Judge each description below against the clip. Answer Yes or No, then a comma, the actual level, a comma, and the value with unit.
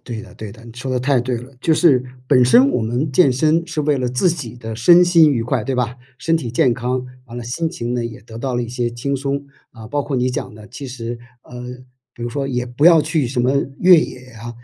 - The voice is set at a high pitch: No, low, 125 Hz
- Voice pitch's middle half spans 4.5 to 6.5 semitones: No, average, 3.3 semitones